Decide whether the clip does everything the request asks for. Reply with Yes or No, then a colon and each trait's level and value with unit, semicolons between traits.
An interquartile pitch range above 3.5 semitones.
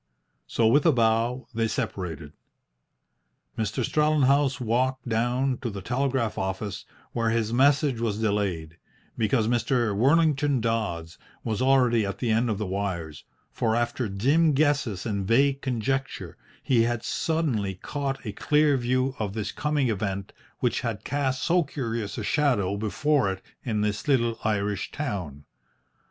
Yes: average, 4.6 semitones